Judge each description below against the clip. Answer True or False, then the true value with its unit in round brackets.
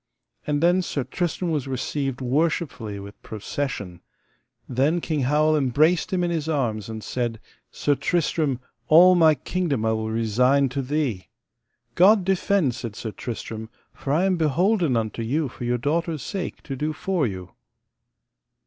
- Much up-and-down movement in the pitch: True (5.7 semitones)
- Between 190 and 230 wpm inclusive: False (155 wpm)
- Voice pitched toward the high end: False (140 Hz)